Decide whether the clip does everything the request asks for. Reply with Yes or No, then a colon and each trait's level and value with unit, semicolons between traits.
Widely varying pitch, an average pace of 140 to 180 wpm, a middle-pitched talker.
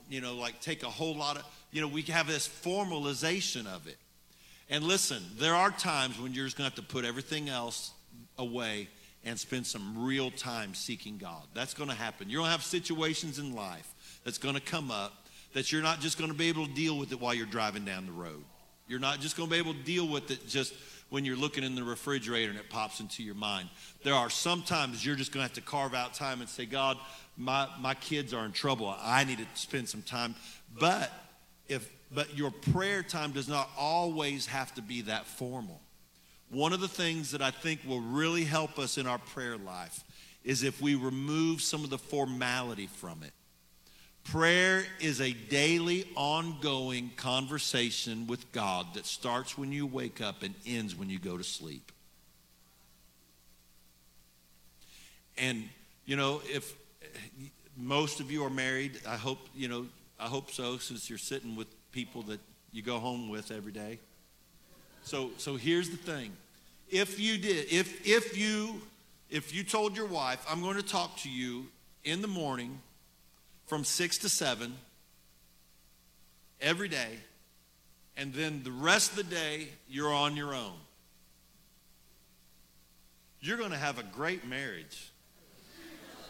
No: wide, 5.7 semitones; average, 175 wpm; low, 130 Hz